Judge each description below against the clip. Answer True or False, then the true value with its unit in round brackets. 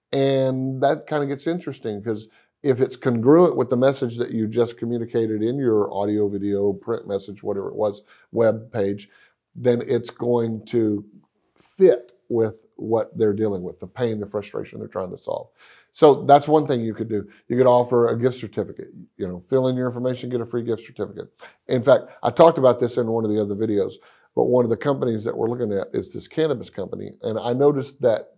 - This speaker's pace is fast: True (210 wpm)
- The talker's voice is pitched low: True (120 Hz)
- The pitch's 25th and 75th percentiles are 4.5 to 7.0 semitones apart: False (3.2 semitones)